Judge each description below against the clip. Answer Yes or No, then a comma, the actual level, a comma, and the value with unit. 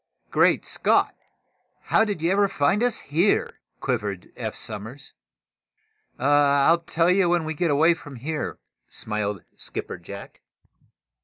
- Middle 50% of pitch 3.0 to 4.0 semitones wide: No, average, 5.1 semitones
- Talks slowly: Yes, slow, 130 wpm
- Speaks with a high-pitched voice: No, medium, 150 Hz